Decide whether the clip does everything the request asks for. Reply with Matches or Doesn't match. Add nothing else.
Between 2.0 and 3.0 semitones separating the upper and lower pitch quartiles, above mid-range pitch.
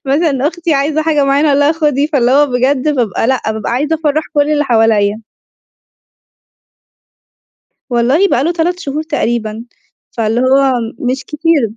Doesn't match